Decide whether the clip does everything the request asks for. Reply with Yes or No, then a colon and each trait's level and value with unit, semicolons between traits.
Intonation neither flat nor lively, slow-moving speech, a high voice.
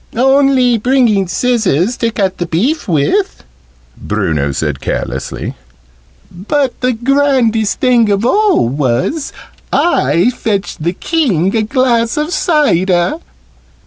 No: wide, 6.9 semitones; slow, 110 wpm; high, 230 Hz